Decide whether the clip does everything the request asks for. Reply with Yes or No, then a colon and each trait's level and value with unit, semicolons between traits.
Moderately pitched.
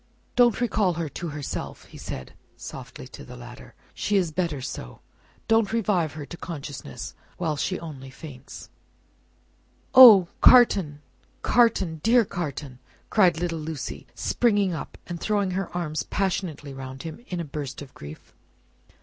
Yes: medium, 170 Hz